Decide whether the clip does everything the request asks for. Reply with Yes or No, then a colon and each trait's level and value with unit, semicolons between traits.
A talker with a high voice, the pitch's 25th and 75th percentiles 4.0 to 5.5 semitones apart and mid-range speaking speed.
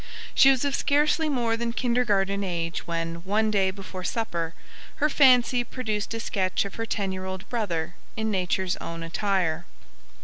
Yes: high, 200 Hz; average, 4.5 semitones; average, 165 wpm